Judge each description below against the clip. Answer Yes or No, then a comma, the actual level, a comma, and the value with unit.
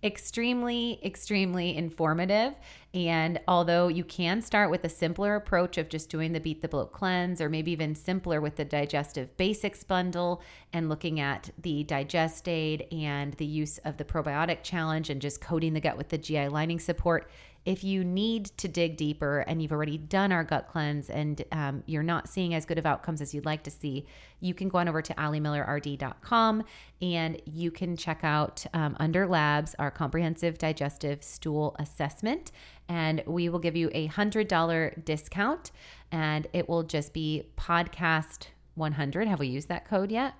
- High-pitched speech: No, medium, 160 Hz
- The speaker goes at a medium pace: Yes, average, 180 wpm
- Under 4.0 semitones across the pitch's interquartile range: Yes, average, 2.7 semitones